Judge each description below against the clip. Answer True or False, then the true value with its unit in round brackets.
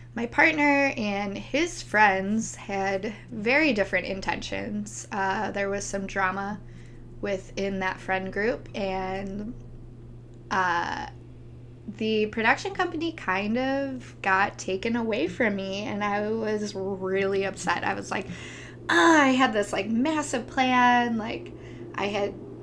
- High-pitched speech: True (200 Hz)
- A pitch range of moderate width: True (3.9 semitones)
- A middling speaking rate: False (125 wpm)